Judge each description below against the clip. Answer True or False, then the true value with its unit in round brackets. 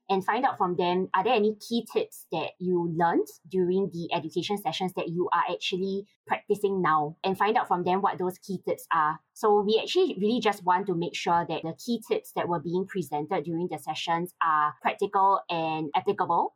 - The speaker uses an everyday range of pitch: True (3.0 semitones)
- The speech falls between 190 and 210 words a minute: True (205 wpm)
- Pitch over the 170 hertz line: True (185 Hz)